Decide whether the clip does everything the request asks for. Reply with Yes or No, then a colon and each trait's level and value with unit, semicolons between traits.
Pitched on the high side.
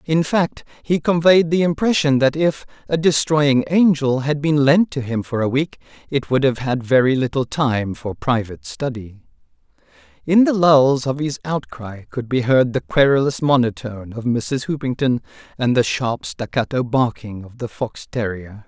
No: low, 135 Hz